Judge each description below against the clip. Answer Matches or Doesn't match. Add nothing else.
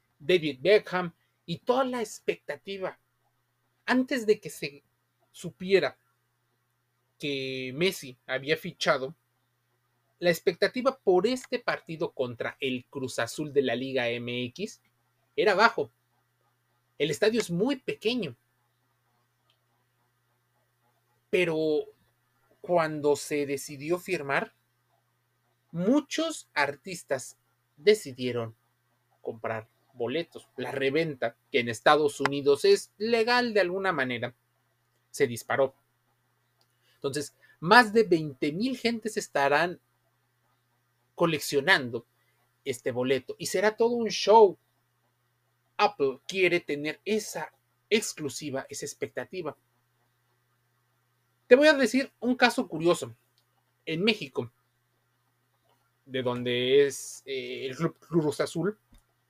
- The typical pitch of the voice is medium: Matches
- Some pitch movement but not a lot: Doesn't match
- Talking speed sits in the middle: Doesn't match